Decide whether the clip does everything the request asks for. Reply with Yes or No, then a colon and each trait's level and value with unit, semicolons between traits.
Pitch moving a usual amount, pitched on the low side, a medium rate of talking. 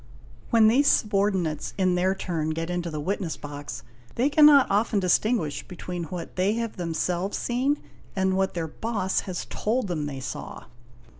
No: average, 4.5 semitones; high, 190 Hz; average, 165 wpm